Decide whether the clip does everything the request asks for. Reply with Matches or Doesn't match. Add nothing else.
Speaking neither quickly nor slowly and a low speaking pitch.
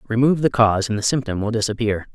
Doesn't match